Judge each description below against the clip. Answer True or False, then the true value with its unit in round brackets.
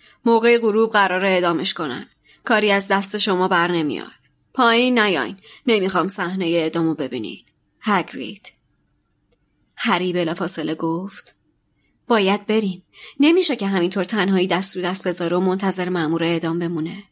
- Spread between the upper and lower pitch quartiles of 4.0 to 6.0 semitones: False (3.4 semitones)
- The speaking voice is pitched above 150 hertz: True (185 Hz)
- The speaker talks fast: False (130 wpm)